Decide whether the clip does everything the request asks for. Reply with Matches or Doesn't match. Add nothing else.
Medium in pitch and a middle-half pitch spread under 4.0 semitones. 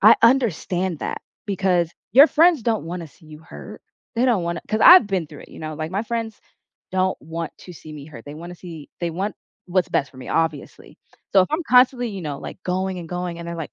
Doesn't match